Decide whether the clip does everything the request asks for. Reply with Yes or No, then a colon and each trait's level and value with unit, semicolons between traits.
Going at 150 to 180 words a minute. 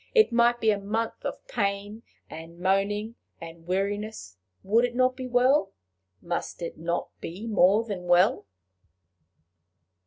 No: slow, 135 wpm